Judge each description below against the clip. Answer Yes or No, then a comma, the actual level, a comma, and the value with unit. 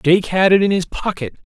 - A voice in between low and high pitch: Yes, medium, 180 Hz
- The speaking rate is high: Yes, fast, 240 wpm